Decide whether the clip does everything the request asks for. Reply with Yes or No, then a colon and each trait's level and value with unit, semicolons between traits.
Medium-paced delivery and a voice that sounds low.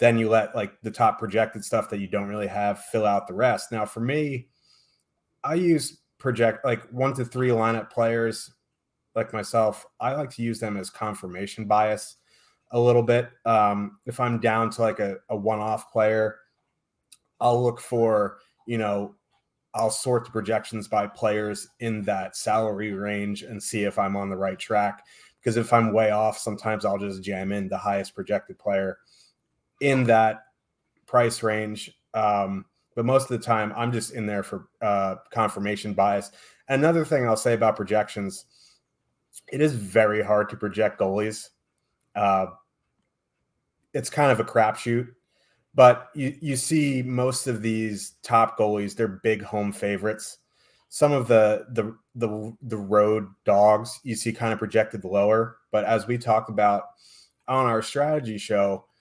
Yes: average, 165 wpm; low, 110 Hz